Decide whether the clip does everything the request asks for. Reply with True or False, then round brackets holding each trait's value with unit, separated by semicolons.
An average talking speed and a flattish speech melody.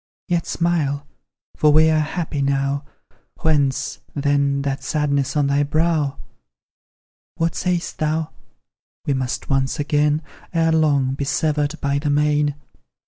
False (130 wpm; 2.0 semitones)